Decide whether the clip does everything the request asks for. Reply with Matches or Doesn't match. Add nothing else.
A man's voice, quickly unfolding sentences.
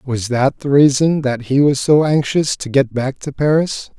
Matches